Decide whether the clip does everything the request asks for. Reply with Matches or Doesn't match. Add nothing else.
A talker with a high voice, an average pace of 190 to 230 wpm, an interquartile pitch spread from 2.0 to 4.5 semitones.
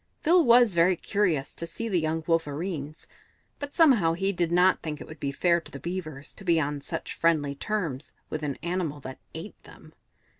Doesn't match